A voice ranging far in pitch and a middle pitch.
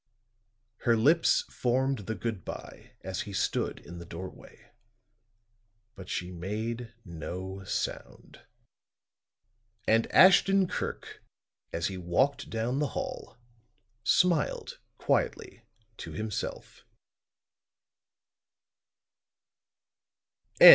No: wide, 6.1 semitones; low, 110 Hz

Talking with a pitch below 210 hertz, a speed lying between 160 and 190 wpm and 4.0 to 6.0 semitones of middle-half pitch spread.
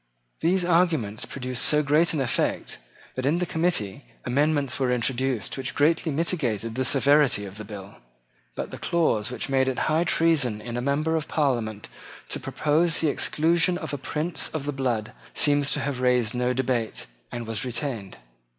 Yes: low, 135 Hz; average, 175 wpm; average, 4.6 semitones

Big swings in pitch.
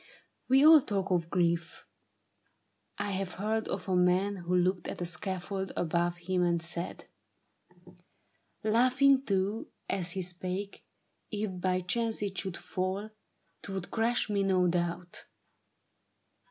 No: narrow, 2.6 semitones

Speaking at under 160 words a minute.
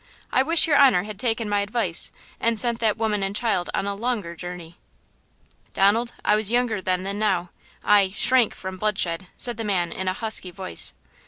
No: average, 185 wpm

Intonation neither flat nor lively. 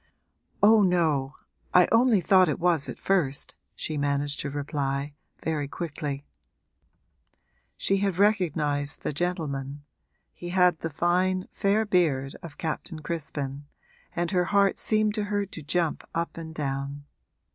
Yes: average, 4.4 semitones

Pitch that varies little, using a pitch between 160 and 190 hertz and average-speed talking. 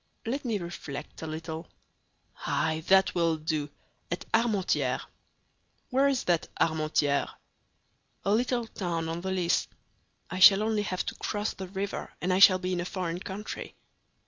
No: average, 4.0 semitones; medium, 185 Hz; average, 150 wpm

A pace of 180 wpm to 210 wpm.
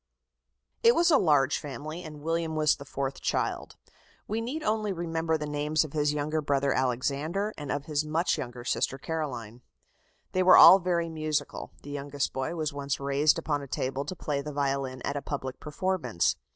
Yes: average, 185 wpm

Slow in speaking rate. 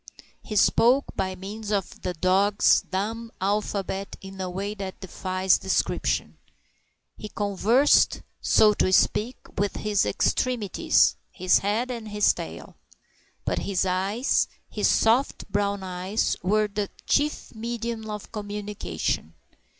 Yes: slow, 125 wpm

